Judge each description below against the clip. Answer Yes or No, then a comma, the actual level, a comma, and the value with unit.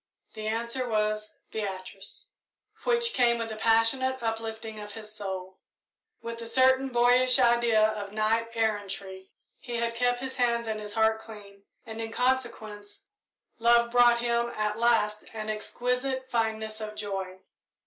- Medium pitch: No, high, 225 Hz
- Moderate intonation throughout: No, narrow, 2.1 semitones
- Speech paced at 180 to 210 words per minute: No, average, 145 wpm